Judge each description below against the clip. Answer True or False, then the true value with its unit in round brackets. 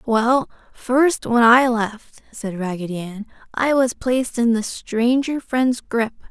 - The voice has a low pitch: False (235 Hz)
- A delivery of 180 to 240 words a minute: False (150 wpm)